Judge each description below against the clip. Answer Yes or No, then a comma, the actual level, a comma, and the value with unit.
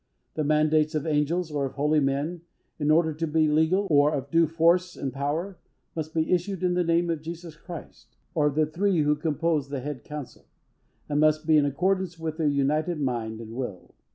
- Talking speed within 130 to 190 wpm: No, fast, 205 wpm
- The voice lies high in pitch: No, medium, 155 Hz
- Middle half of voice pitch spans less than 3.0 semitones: Yes, narrow, 2.4 semitones